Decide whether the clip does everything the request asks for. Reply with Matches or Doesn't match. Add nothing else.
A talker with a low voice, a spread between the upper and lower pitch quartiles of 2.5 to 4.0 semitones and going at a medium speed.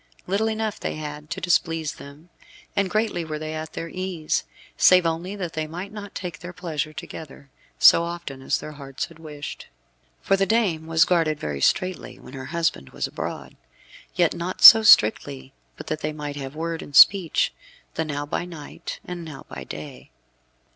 Doesn't match